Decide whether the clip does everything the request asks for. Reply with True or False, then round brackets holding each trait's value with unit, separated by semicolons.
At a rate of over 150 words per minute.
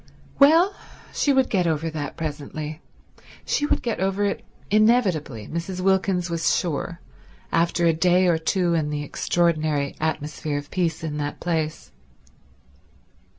False (140 wpm)